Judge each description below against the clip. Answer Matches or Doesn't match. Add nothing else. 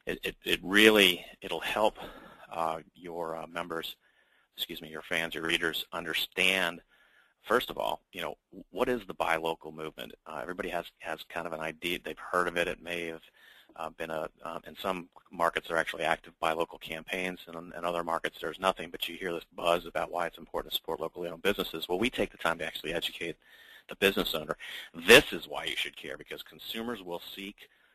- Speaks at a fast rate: Matches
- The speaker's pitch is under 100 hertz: Matches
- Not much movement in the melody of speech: Matches